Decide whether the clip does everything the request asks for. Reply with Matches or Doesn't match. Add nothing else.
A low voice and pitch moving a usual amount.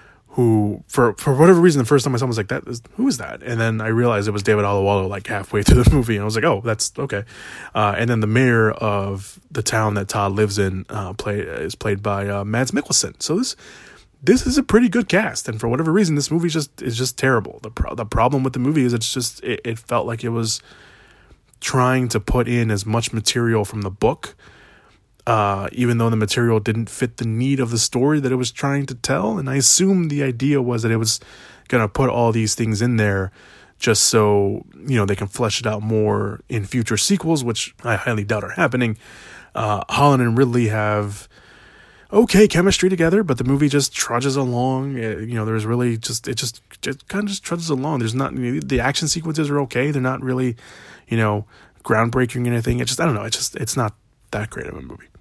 Matches